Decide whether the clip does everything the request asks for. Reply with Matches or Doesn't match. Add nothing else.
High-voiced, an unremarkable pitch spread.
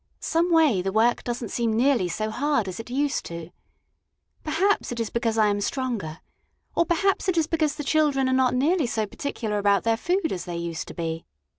Doesn't match